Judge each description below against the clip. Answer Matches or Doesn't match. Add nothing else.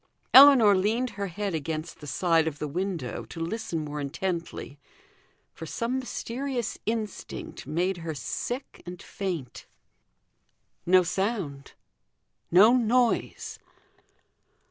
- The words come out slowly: Matches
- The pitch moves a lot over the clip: Matches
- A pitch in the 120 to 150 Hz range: Doesn't match